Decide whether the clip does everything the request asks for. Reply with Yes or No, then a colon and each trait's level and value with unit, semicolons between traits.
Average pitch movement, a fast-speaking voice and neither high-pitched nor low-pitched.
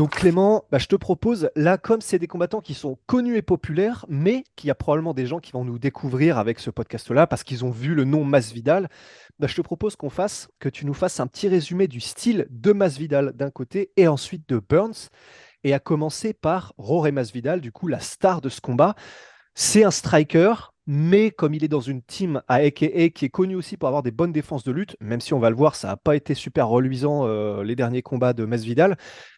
No: wide, 6.0 semitones; fast, 235 wpm; medium, 150 Hz